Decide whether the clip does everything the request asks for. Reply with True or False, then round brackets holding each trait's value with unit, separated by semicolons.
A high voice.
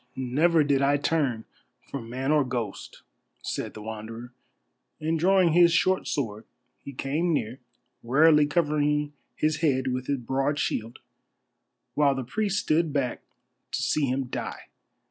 False (140 Hz)